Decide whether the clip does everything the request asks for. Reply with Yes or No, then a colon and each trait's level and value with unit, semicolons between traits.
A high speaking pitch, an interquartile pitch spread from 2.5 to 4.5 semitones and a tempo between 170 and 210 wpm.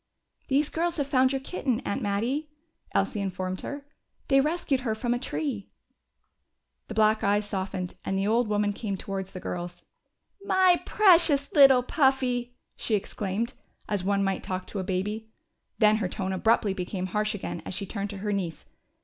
No: high, 215 Hz; wide, 5.4 semitones; average, 175 wpm